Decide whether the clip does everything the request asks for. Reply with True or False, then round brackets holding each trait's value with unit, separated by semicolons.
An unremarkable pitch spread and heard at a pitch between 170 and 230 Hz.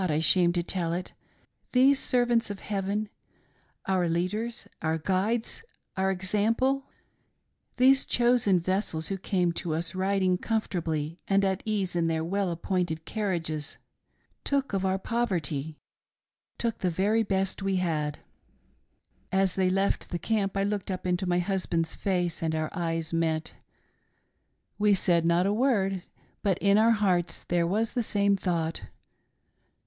True (3.3 semitones; 190 Hz)